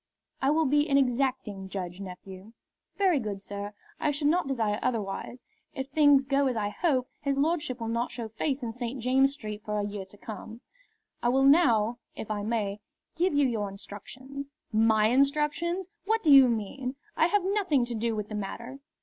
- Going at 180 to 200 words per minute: Yes, average, 190 wpm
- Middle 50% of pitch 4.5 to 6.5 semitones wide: Yes, average, 4.8 semitones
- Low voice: No, very high, 250 Hz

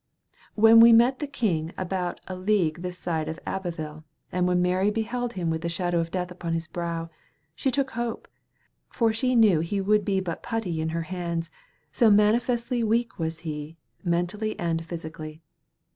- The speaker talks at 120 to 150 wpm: No, average, 175 wpm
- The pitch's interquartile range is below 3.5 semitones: No, average, 5.0 semitones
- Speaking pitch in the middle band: Yes, medium, 180 Hz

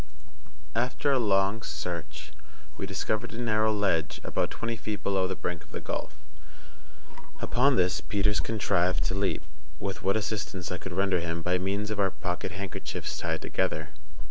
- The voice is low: Yes, very low, 95 Hz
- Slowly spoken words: No, average, 165 wpm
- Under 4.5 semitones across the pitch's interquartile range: Yes, average, 3.1 semitones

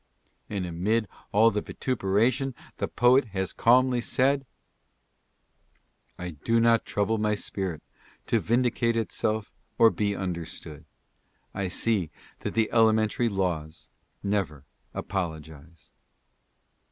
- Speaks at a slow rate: Yes, slow, 110 wpm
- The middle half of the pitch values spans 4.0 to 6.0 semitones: Yes, average, 4.3 semitones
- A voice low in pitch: Yes, low, 105 Hz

